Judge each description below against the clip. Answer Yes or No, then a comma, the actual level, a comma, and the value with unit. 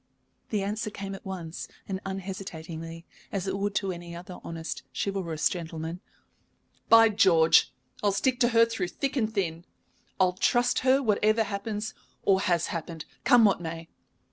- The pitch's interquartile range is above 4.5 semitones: No, average, 3.9 semitones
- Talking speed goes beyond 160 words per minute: No, average, 155 wpm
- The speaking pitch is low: No, high, 195 Hz